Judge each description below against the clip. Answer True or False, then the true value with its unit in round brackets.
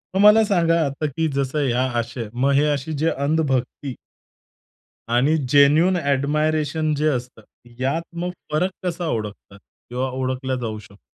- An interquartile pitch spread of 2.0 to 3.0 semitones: False (3.8 semitones)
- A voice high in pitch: False (140 Hz)